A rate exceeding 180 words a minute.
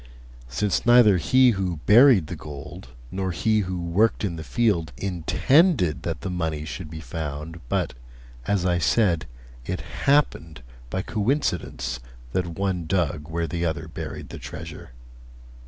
No: average, 145 wpm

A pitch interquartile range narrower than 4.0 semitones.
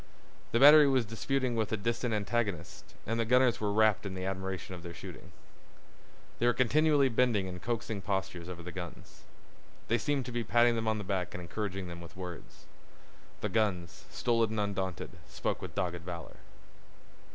No: average, 4.3 semitones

